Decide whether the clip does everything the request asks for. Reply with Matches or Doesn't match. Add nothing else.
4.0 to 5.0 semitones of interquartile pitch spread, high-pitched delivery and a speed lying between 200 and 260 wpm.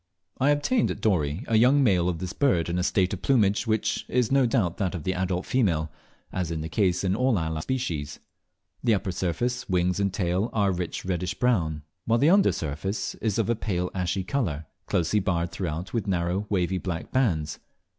Doesn't match